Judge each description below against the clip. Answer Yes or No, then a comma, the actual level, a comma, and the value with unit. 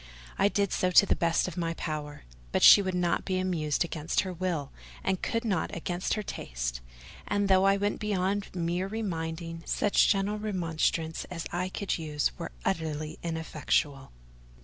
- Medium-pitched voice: Yes, medium, 175 Hz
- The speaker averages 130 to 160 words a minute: No, average, 170 wpm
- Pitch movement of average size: Yes, average, 3.3 semitones